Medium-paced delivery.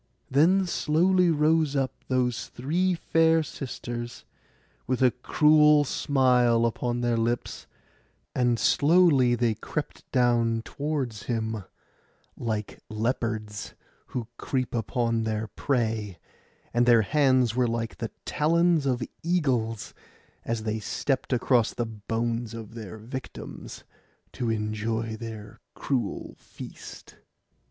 No: slow, 115 wpm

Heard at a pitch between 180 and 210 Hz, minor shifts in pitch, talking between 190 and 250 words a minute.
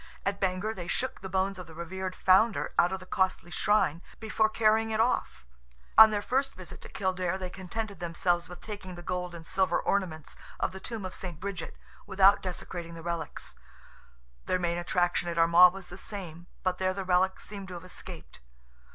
Yes: medium, 185 Hz; narrow, 2.3 semitones; average, 195 wpm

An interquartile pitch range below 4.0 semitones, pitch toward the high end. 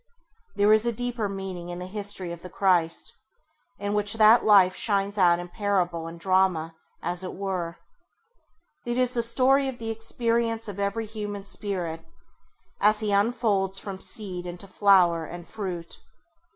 Yes: average, 3.4 semitones; high, 200 Hz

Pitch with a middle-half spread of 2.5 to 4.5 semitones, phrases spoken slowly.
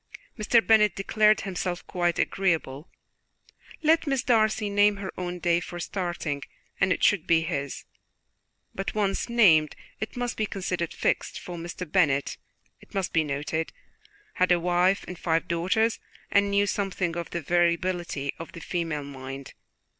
No: average, 3.5 semitones; average, 155 wpm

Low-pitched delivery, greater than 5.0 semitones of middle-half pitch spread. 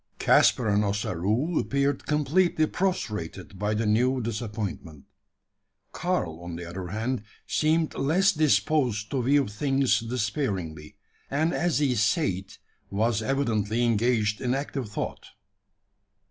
Yes: low, 115 Hz; wide, 5.4 semitones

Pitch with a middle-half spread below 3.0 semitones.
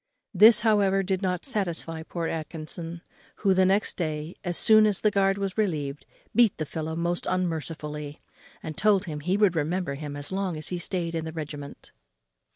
No: average, 3.7 semitones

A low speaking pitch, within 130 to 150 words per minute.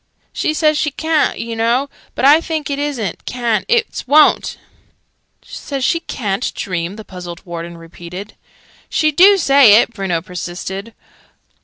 No: high, 235 Hz; average, 145 wpm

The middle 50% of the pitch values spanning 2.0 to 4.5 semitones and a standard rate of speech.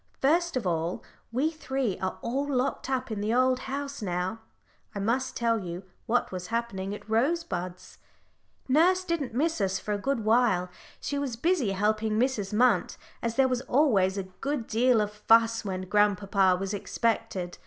No: average, 5.1 semitones; average, 170 wpm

